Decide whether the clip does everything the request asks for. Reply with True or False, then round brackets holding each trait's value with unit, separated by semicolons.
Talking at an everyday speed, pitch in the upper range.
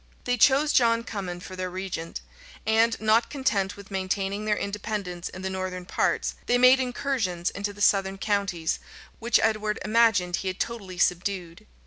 True (160 wpm; 200 Hz)